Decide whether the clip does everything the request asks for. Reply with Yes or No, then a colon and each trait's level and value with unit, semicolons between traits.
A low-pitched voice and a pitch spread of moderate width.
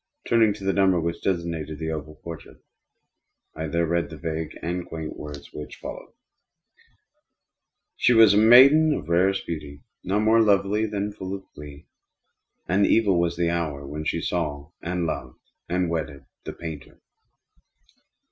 Yes: very low, 85 Hz; average, 4.1 semitones